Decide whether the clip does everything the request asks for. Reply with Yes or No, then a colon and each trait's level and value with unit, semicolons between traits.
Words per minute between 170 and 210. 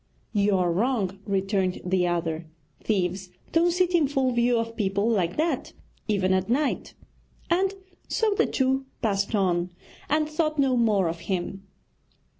No: average, 150 wpm